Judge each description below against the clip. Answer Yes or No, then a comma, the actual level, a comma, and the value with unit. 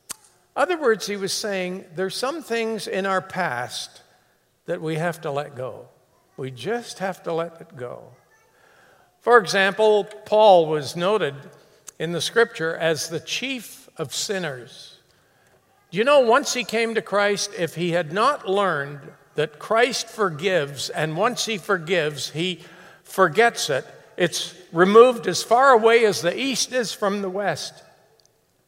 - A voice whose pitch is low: No, high, 190 Hz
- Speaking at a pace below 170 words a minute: Yes, average, 150 wpm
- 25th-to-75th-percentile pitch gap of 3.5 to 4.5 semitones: No, average, 5.1 semitones